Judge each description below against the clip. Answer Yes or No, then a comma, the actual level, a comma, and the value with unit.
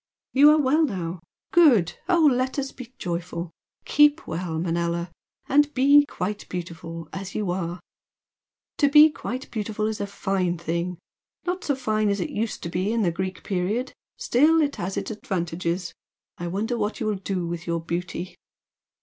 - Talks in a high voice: Yes, high, 195 Hz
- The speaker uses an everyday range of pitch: No, wide, 6.9 semitones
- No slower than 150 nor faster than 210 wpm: Yes, average, 170 wpm